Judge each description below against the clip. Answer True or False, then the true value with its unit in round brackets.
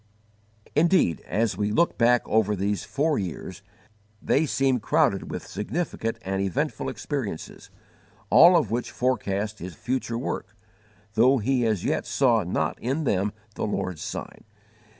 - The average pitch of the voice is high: False (115 Hz)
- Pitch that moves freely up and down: False (4.8 semitones)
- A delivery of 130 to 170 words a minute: True (140 wpm)